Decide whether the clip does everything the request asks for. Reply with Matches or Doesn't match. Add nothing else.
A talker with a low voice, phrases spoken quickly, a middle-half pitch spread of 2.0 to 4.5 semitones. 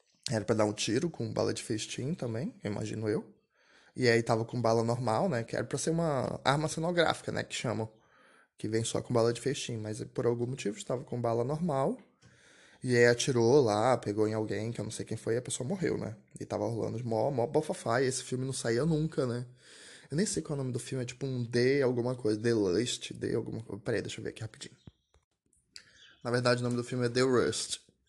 Matches